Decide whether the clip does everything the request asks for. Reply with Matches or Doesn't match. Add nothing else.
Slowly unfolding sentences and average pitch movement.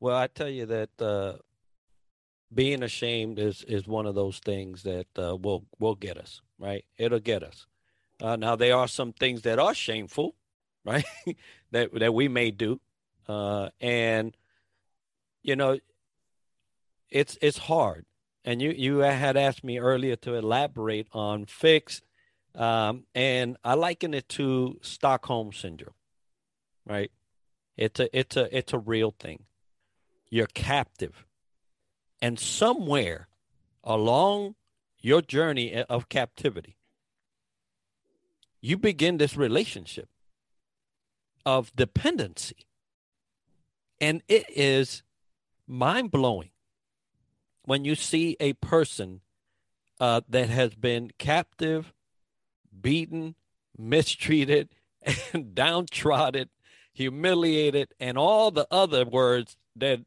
Matches